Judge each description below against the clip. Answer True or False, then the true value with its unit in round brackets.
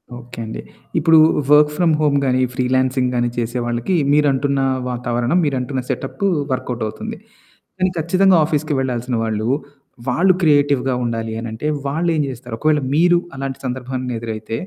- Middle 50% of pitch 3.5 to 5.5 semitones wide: True (3.8 semitones)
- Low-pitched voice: True (130 Hz)